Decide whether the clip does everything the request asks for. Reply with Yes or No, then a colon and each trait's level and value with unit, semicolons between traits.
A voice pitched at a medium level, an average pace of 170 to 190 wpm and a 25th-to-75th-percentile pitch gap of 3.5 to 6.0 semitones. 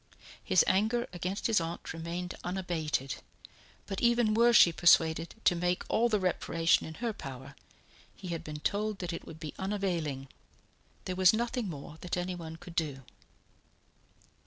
No: medium, 180 Hz; average, 155 wpm; average, 3.8 semitones